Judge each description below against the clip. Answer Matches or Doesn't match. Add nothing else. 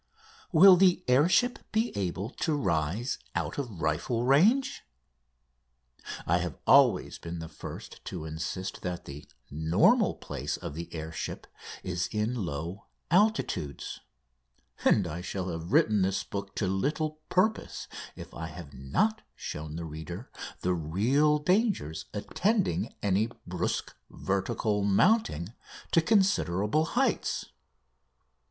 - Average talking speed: Doesn't match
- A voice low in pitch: Matches